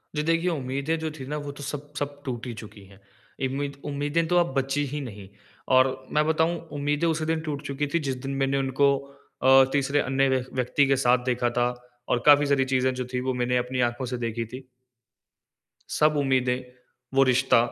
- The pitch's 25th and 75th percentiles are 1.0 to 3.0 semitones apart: Yes, narrow, 2.5 semitones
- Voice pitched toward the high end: No, low, 135 Hz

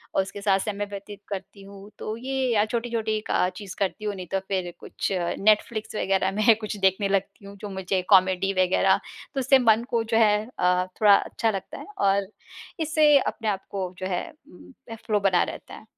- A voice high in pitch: Yes, high, 200 Hz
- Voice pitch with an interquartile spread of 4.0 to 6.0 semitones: No, narrow, 2.4 semitones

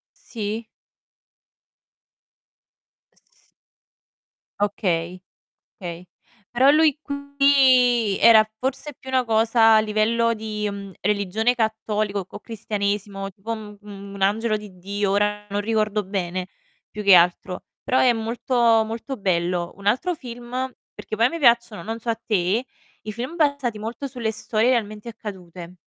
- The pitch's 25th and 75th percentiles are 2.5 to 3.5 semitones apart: Yes, average, 2.9 semitones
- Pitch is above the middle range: Yes, high, 215 Hz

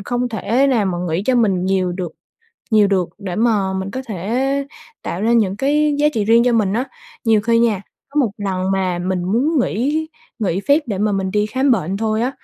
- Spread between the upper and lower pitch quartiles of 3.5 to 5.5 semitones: Yes, average, 4.4 semitones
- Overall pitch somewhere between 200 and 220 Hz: Yes, high, 215 Hz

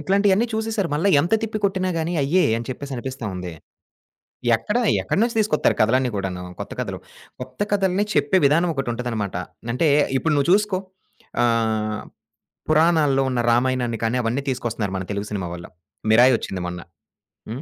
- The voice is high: No, low, 130 Hz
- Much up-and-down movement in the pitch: Yes, wide, 8.0 semitones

